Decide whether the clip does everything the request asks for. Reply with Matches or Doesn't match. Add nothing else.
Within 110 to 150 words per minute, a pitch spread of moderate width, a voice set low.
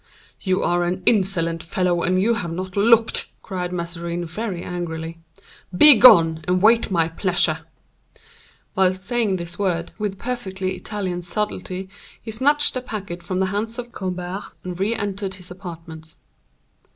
Doesn't match